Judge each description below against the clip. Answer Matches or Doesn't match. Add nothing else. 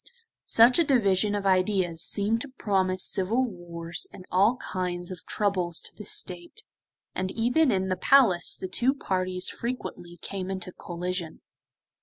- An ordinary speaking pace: Matches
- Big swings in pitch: Doesn't match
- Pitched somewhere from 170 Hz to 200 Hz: Matches